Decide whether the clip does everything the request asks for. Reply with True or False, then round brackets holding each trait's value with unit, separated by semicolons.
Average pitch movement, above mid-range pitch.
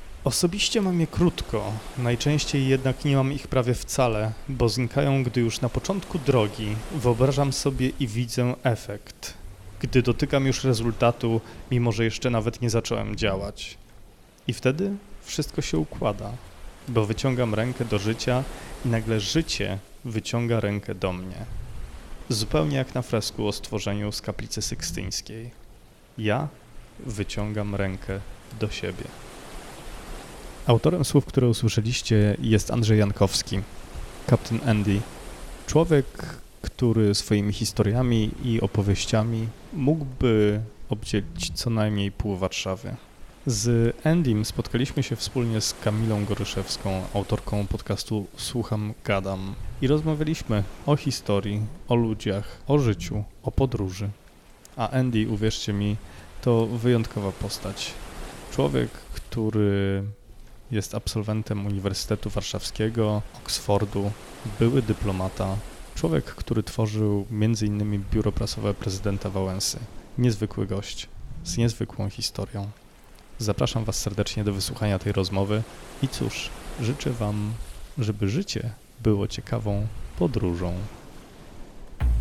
False (3.3 semitones; 110 Hz)